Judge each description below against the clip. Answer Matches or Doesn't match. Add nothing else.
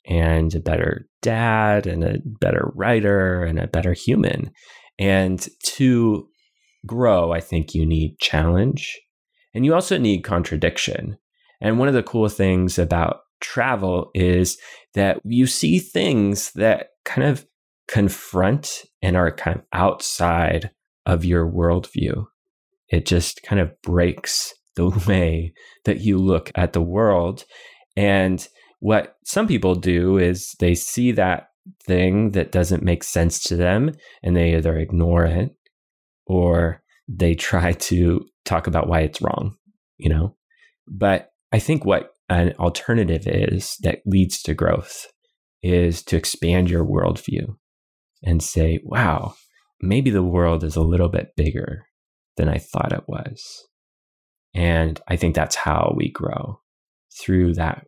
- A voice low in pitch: Matches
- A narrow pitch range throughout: Doesn't match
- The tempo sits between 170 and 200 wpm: Doesn't match